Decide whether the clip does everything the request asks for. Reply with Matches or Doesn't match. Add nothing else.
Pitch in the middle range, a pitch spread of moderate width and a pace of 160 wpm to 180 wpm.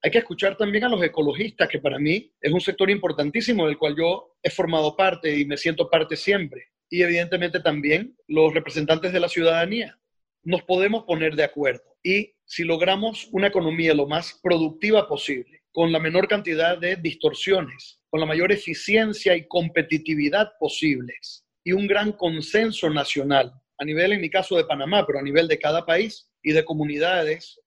Matches